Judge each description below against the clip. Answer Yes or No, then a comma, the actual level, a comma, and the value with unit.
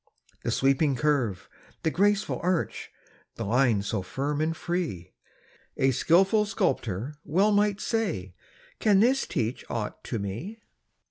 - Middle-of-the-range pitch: Yes, medium, 150 Hz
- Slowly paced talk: Yes, slow, 130 wpm